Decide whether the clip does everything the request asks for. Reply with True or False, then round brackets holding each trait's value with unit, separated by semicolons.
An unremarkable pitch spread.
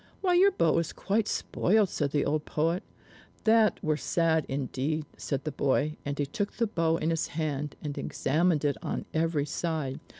True (3.0 semitones)